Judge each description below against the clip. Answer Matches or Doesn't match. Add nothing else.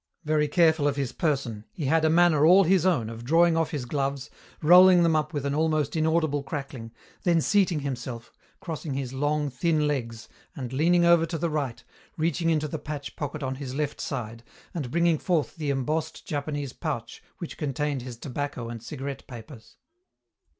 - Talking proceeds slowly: Doesn't match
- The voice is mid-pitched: Matches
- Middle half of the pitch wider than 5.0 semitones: Doesn't match